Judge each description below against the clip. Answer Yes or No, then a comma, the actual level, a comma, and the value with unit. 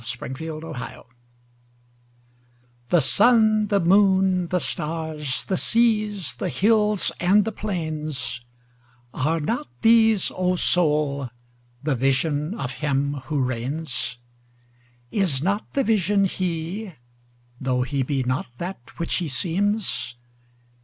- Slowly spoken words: Yes, slow, 110 wpm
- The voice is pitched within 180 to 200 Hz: No, medium, 160 Hz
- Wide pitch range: Yes, wide, 7.1 semitones